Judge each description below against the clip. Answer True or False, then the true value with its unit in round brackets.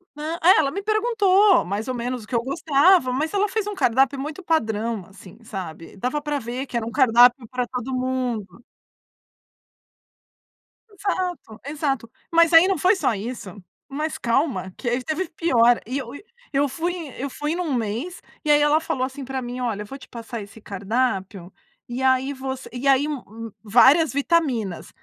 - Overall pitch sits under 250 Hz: False (260 Hz)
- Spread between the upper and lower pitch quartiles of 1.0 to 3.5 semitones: False (5.2 semitones)